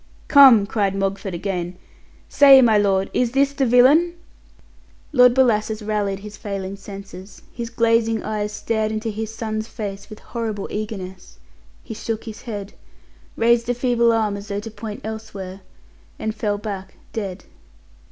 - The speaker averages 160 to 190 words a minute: No, average, 150 wpm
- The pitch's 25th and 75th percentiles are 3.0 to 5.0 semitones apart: No, narrow, 2.6 semitones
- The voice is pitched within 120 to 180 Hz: No, high, 215 Hz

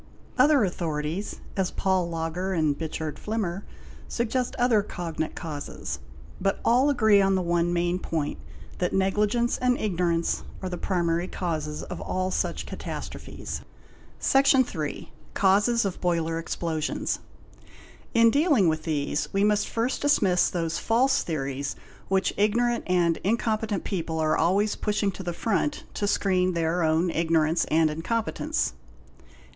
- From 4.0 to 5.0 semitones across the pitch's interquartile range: Yes, average, 4.5 semitones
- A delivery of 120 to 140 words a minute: Yes, slow, 135 wpm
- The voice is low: No, medium, 185 Hz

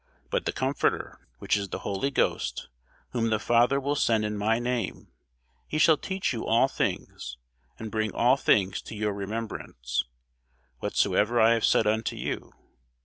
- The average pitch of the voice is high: No, low, 110 Hz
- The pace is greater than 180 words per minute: No, average, 160 wpm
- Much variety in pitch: No, average, 2.9 semitones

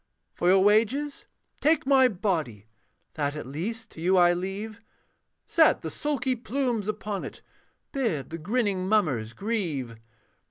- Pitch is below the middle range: No, high, 200 Hz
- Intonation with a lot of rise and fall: Yes, wide, 6.0 semitones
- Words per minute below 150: Yes, slow, 135 wpm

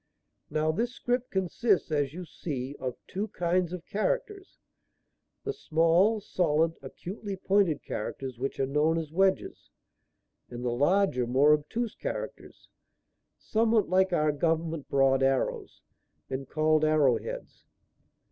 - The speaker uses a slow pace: Yes, slow, 130 wpm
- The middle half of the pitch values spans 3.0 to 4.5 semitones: No, wide, 5.4 semitones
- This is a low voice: No, medium, 165 Hz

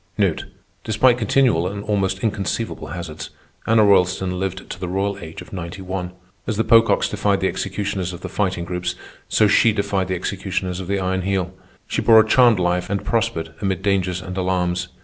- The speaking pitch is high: No, very low, 95 Hz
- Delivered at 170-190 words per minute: Yes, average, 185 wpm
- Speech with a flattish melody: Yes, narrow, 2.3 semitones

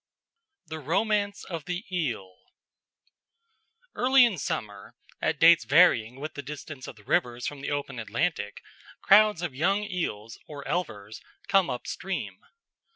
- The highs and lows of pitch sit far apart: Yes, wide, 7.2 semitones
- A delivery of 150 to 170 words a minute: No, average, 140 wpm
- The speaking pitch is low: No, medium, 150 Hz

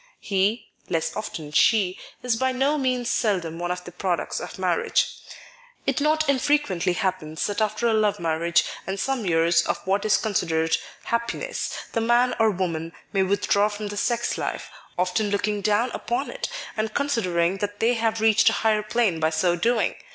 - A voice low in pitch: No, high, 210 Hz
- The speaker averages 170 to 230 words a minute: Yes, average, 180 wpm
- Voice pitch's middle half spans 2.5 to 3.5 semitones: No, average, 4.6 semitones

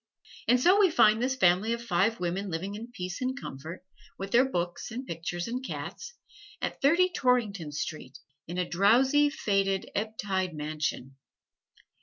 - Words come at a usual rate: Yes, average, 160 wpm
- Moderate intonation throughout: No, wide, 6.3 semitones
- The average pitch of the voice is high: Yes, high, 200 Hz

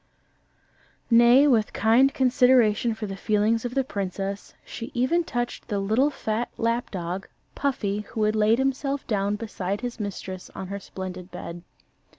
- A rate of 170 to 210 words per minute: No, average, 155 wpm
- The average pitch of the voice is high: Yes, high, 220 Hz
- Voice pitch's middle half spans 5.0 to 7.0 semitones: No, average, 3.8 semitones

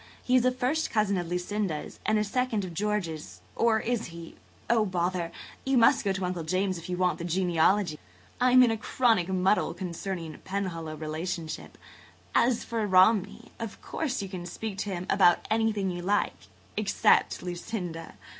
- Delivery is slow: No, average, 170 wpm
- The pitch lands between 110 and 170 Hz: No, high, 190 Hz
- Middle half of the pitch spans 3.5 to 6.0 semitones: Yes, average, 3.9 semitones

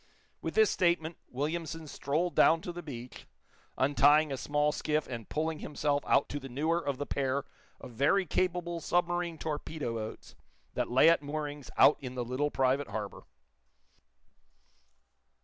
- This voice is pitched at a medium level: Yes, medium, 150 Hz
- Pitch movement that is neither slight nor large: Yes, average, 3.5 semitones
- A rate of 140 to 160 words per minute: Yes, average, 150 wpm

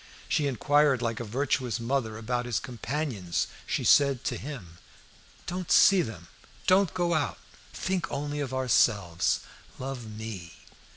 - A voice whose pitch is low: Yes, low, 125 Hz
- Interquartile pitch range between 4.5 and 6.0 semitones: Yes, average, 4.8 semitones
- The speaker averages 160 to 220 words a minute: No, slow, 135 wpm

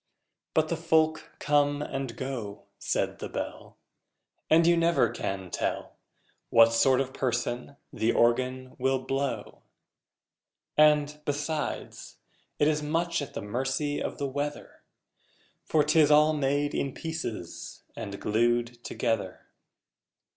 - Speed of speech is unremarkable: No, slow, 125 wpm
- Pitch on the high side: No, medium, 140 Hz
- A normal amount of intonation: Yes, average, 3.8 semitones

